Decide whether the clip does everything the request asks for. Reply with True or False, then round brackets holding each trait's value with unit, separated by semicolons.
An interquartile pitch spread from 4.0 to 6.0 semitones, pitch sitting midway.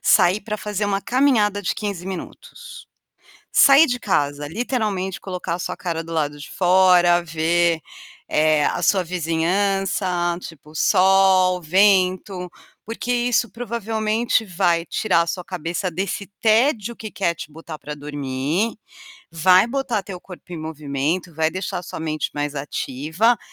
True (4.3 semitones; 180 Hz)